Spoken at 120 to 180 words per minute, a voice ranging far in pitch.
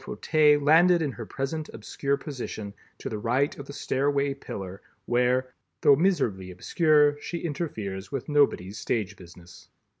Yes: average, 145 wpm; wide, 5.8 semitones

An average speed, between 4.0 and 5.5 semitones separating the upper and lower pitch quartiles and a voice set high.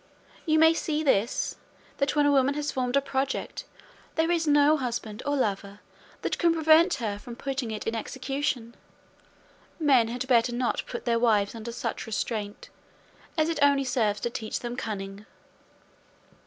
Yes: average, 170 wpm; average, 4.3 semitones; very high, 255 Hz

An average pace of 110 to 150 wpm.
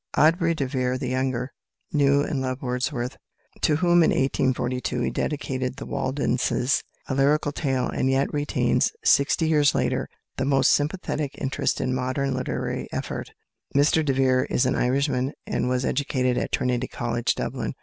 No: average, 160 wpm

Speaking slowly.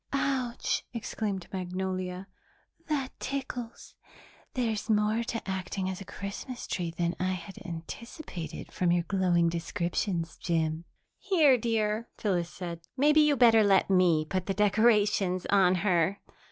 Yes: slow, 130 wpm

